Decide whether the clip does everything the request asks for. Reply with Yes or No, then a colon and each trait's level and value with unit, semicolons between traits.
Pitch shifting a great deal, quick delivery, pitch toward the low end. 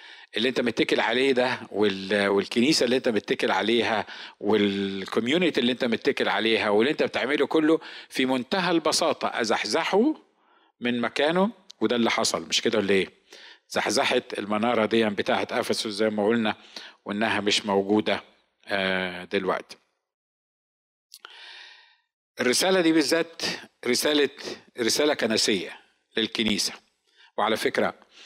No: wide, 5.9 semitones; average, 115 wpm; low, 110 Hz